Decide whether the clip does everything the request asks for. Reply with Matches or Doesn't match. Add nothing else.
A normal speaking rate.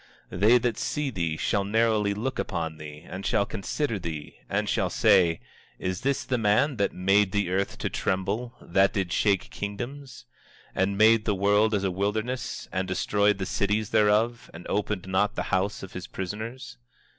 Matches